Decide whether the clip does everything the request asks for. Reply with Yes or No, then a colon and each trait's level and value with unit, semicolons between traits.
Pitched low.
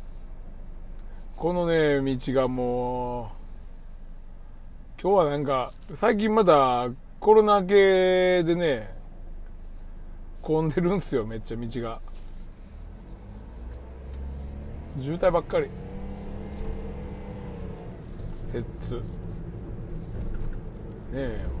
Yes: low, 110 Hz